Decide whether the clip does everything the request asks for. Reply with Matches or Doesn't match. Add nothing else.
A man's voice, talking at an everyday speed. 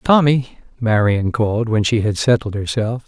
Matches